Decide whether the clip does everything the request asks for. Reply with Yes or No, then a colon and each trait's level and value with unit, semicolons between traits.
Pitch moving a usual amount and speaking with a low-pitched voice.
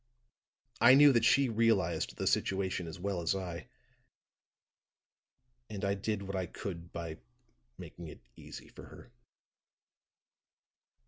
Yes: average, 4.5 semitones; very low, 95 Hz